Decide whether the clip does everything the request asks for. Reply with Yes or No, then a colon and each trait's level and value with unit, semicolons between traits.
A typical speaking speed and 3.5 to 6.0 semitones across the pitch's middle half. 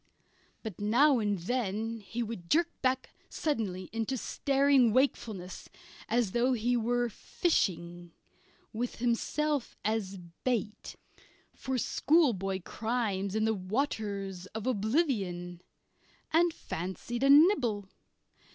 No: slow, 105 wpm; average, 4.7 semitones